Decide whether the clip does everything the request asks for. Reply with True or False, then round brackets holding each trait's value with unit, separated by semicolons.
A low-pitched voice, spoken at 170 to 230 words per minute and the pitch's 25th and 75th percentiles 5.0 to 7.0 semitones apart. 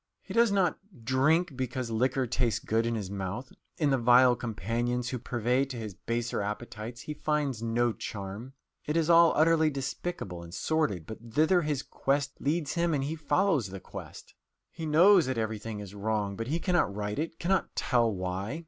True (125 Hz; 185 wpm; 5.6 semitones)